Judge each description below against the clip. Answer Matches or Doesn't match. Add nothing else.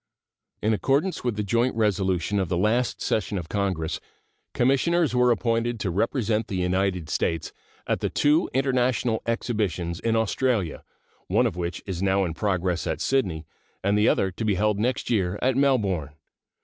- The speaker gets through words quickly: Doesn't match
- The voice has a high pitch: Doesn't match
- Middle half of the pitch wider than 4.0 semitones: Matches